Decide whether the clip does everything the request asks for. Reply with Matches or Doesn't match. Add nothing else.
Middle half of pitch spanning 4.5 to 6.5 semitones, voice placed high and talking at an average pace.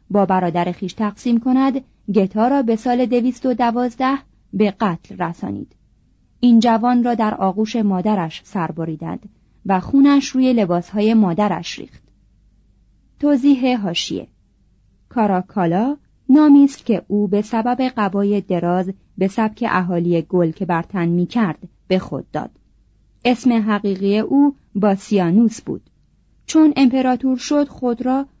Matches